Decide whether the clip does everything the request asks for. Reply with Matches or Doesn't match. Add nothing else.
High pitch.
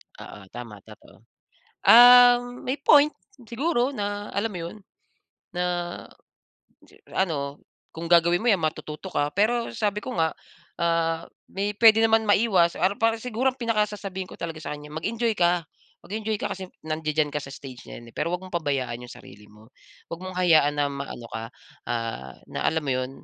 Doesn't match